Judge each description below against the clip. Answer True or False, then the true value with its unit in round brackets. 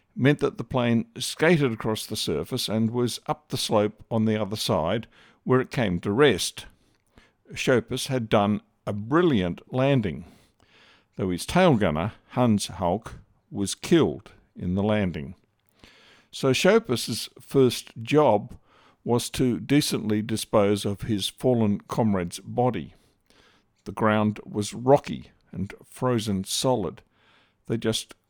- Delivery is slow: True (130 wpm)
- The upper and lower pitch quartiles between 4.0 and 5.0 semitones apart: False (3.3 semitones)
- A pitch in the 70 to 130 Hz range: True (115 Hz)